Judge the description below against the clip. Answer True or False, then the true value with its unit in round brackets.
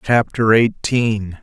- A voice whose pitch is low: True (110 Hz)